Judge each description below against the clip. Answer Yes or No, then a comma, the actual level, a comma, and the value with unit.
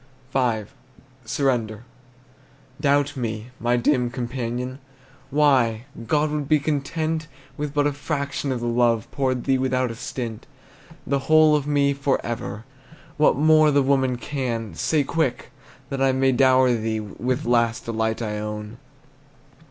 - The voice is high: No, low, 130 Hz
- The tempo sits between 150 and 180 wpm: No, average, 140 wpm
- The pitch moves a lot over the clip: No, average, 3.4 semitones